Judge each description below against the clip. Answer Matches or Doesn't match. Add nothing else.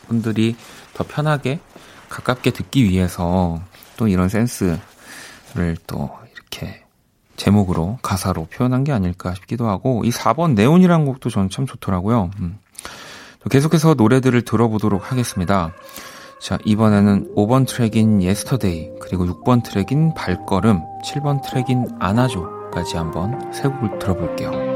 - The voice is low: Matches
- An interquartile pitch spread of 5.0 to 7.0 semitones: Matches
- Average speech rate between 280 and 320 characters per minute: Matches